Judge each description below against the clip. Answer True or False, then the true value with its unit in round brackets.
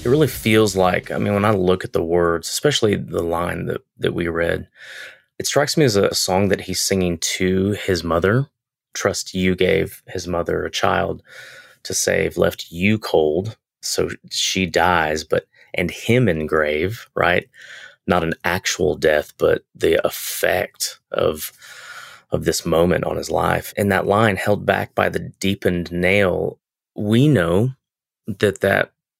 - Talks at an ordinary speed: True (160 wpm)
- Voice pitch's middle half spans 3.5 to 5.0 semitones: False (3.1 semitones)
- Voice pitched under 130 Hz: True (95 Hz)